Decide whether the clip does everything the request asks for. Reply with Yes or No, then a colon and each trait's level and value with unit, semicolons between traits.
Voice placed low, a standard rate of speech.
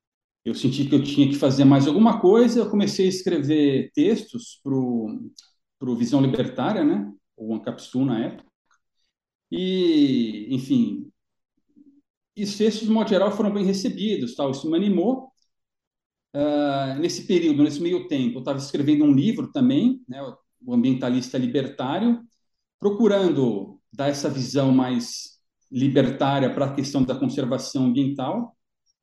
No: medium, 170 Hz; average, 140 wpm